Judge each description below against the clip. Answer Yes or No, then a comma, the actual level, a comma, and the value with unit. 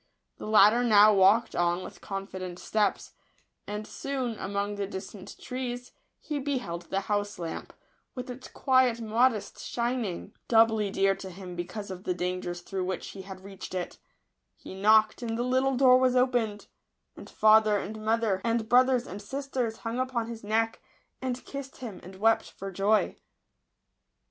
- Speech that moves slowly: No, average, 160 wpm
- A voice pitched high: Yes, high, 215 Hz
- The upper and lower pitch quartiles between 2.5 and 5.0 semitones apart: Yes, average, 4.0 semitones